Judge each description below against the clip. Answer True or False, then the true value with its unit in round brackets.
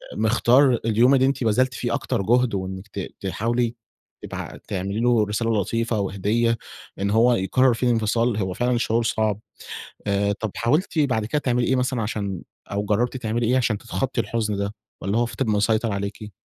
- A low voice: True (115 Hz)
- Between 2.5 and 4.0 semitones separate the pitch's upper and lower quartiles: True (2.9 semitones)